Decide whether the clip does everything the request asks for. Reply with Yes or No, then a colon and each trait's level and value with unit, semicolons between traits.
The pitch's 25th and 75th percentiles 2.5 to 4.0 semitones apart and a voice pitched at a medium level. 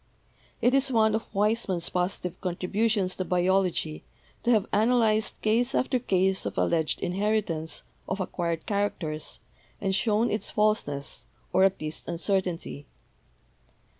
No: average, 3.6 semitones; high, 195 Hz